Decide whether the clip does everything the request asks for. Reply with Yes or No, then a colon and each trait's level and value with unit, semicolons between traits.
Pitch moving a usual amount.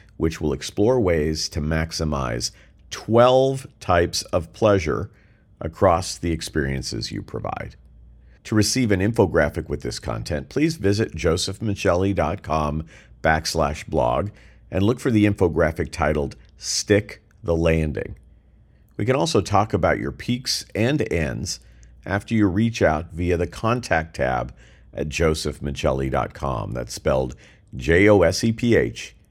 No: wide, 5.8 semitones